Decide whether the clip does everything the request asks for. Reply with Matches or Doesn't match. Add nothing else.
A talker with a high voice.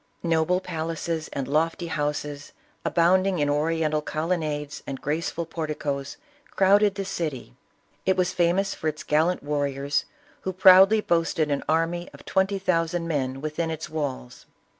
Doesn't match